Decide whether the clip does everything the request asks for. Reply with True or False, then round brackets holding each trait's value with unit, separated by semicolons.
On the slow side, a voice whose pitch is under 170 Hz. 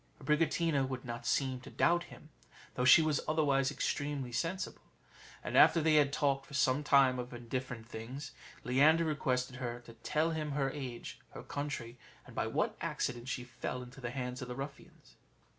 False (175 wpm; 135 Hz)